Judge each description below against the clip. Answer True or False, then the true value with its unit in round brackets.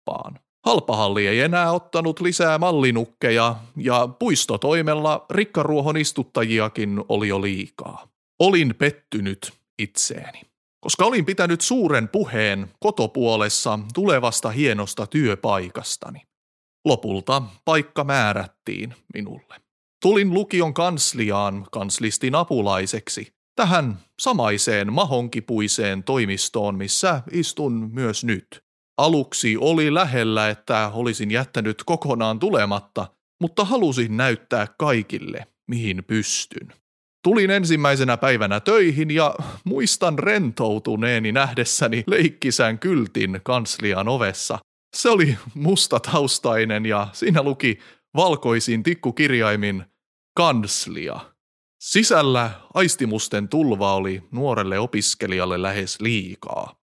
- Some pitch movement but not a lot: False (6.3 semitones)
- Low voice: True (120 Hz)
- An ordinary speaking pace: False (90 wpm)